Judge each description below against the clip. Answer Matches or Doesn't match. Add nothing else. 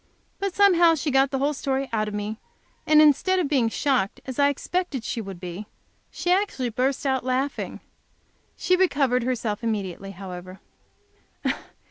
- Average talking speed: Matches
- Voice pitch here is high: Matches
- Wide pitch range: Matches